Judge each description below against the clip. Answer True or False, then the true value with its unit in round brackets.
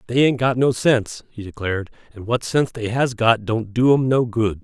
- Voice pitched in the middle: False (115 Hz)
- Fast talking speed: True (235 wpm)